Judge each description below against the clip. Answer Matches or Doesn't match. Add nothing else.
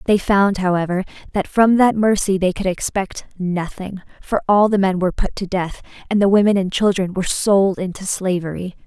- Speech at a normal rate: Matches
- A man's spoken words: Doesn't match